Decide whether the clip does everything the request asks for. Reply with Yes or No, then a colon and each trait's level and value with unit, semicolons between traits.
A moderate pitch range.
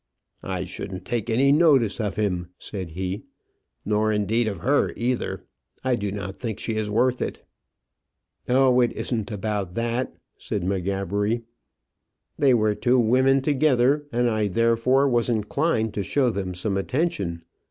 Yes: average, 4.0 semitones